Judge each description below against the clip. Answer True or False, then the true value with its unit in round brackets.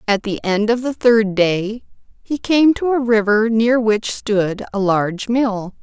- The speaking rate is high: False (185 wpm)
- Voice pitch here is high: True (220 Hz)